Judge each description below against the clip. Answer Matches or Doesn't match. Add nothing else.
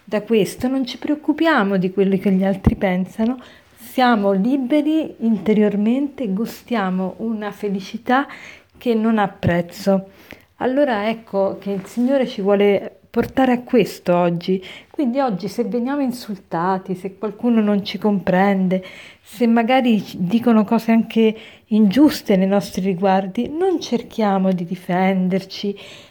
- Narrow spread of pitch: Doesn't match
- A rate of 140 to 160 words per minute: Doesn't match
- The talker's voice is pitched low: Doesn't match